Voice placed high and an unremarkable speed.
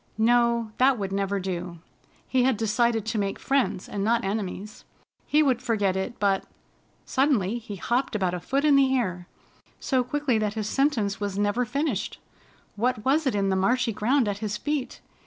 Yes: high, 225 Hz; average, 180 wpm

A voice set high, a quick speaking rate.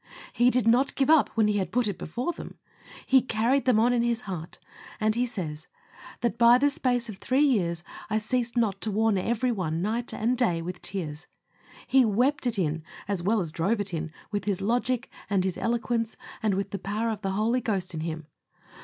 Yes: high, 220 Hz; fast, 210 wpm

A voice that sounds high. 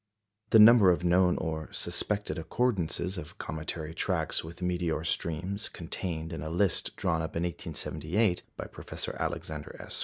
No: very low, 85 Hz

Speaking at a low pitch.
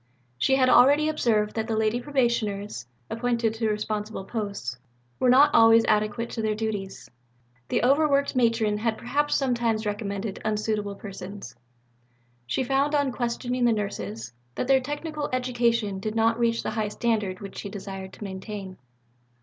No: high, 225 Hz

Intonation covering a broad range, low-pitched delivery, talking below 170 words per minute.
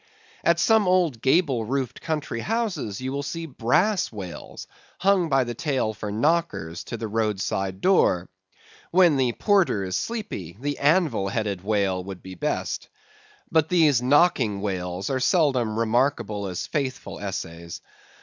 Yes: wide, 8.1 semitones; low, 125 Hz; average, 150 wpm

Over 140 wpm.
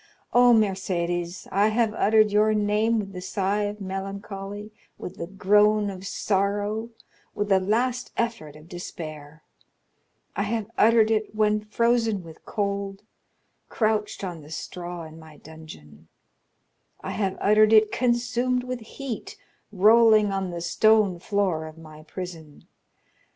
No: slow, 135 wpm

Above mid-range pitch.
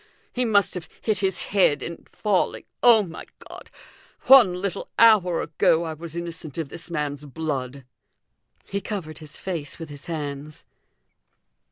No: medium, 170 Hz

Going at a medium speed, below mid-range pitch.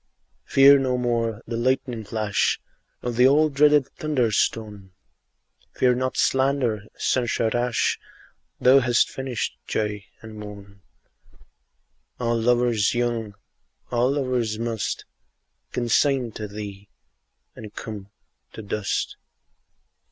No: slow, 105 wpm; low, 120 Hz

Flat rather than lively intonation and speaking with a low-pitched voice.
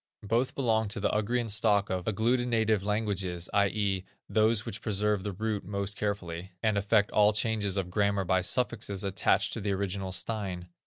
Yes: narrow, 2.2 semitones; low, 100 Hz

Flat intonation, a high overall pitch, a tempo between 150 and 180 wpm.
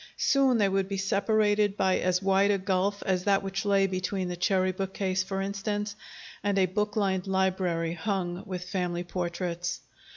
Yes: narrow, 1.6 semitones; high, 195 Hz; average, 170 wpm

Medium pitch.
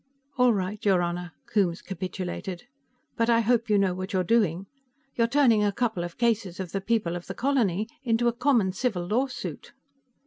No: high, 205 Hz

